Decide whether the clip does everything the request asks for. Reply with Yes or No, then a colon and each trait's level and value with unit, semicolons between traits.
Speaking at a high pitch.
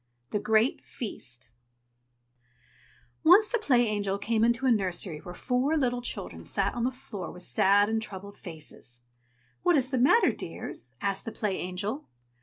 Yes: high, 215 Hz